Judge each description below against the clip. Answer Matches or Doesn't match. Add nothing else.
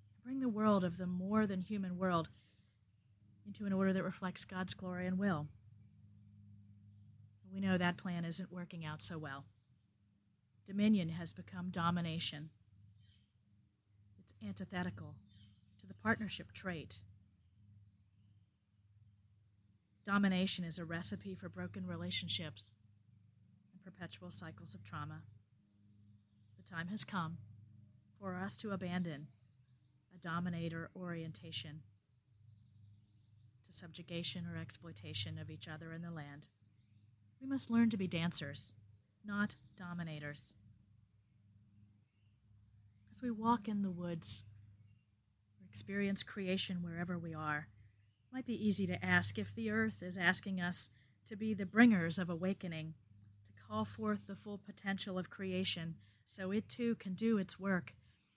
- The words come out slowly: Matches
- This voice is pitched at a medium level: Matches